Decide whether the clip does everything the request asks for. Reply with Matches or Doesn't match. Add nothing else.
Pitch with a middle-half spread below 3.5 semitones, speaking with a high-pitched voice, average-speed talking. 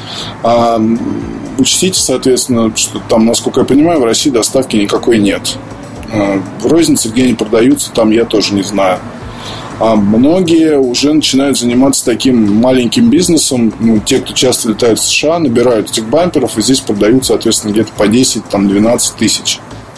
Doesn't match